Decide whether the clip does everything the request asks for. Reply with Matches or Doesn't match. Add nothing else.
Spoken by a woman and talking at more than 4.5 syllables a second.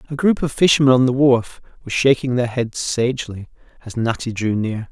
Doesn't match